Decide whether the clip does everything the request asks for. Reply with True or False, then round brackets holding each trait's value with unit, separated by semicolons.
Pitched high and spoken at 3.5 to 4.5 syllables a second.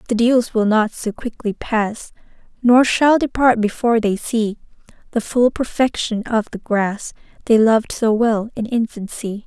True (225 Hz; 4.4 syllables/s)